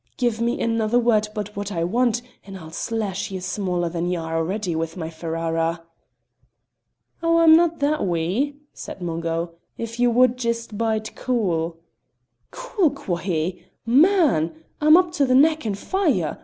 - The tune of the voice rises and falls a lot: Yes, wide, 6.9 semitones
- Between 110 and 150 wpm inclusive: No, average, 165 wpm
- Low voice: No, high, 210 Hz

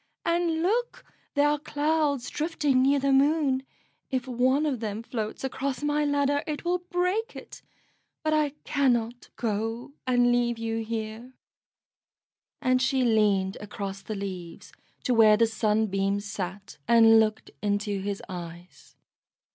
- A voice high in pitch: Yes, high, 245 Hz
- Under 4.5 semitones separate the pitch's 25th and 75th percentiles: No, average, 5.2 semitones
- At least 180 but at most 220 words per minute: No, average, 140 wpm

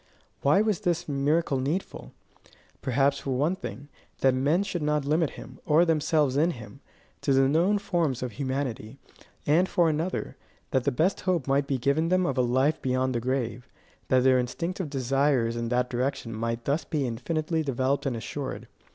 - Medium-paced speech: Yes, average, 175 wpm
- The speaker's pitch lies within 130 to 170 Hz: Yes, medium, 140 Hz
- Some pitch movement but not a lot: Yes, average, 3.9 semitones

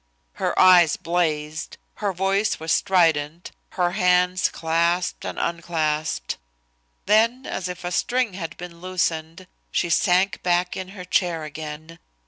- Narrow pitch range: Yes, narrow, 2.2 semitones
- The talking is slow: Yes, slow, 130 wpm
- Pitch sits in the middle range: Yes, medium, 175 Hz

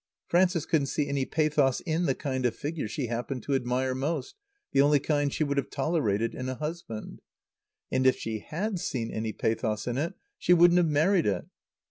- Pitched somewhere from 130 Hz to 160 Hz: Yes, medium, 140 Hz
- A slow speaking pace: No, average, 195 wpm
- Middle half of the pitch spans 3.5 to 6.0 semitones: Yes, average, 4.5 semitones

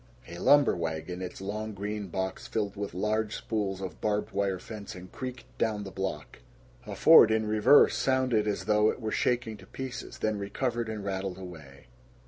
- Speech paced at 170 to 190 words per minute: Yes, average, 175 wpm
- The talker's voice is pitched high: No, low, 105 Hz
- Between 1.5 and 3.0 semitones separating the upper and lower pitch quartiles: Yes, narrow, 2.5 semitones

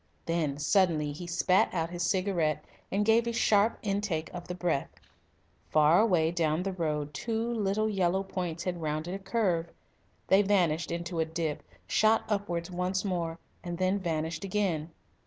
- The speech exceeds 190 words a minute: No, average, 160 wpm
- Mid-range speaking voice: Yes, medium, 175 Hz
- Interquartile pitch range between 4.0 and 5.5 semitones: No, average, 3.3 semitones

